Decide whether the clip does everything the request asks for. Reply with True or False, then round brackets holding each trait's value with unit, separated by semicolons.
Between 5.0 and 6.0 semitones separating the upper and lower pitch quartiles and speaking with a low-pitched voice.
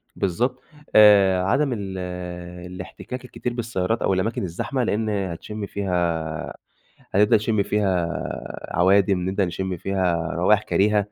False (2.8 semitones; 100 Hz)